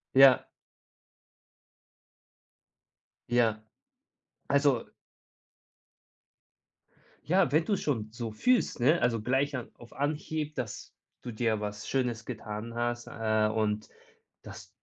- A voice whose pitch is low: Yes, low, 120 Hz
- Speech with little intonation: No, average, 4.4 semitones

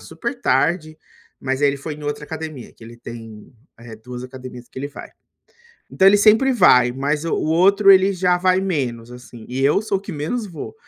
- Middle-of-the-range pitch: Yes, medium, 145 Hz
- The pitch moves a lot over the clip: Yes, wide, 6.6 semitones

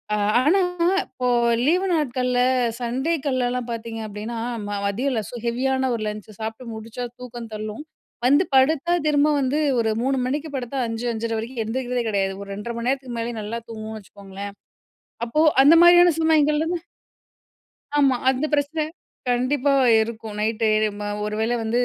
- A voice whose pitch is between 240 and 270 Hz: Yes, high, 245 Hz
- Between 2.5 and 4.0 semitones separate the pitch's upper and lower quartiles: Yes, average, 3.7 semitones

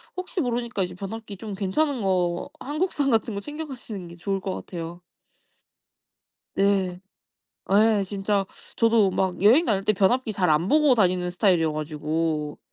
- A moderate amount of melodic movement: Yes, average, 4.3 semitones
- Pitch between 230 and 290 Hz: No, high, 195 Hz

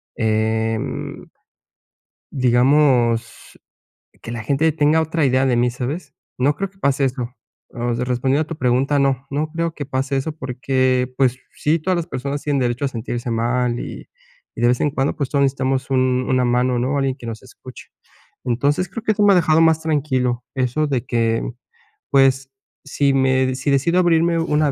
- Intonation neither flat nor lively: Yes, average, 3.1 semitones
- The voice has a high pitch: No, low, 135 Hz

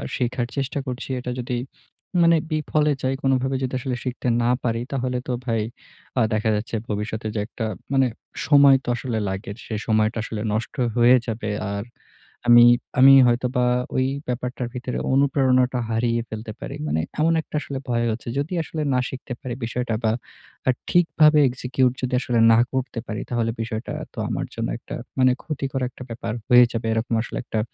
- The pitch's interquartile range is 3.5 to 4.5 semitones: No, narrow, 2.5 semitones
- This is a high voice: No, low, 125 Hz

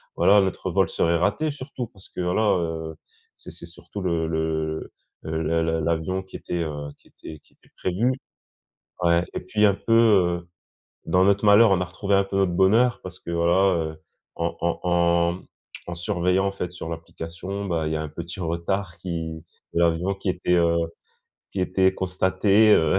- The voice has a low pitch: Yes, very low, 90 Hz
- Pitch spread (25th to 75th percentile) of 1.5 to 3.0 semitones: Yes, average, 2.7 semitones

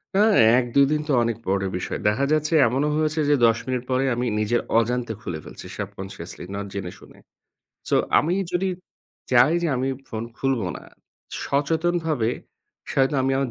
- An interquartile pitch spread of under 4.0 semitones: No, average, 5.2 semitones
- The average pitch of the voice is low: Yes, low, 130 Hz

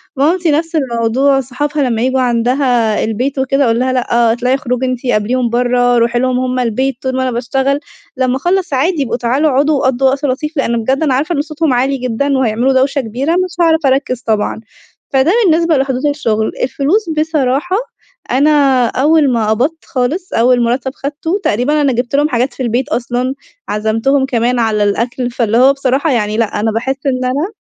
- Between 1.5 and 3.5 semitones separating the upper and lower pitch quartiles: Yes, average, 2.9 semitones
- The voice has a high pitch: Yes, very high, 260 Hz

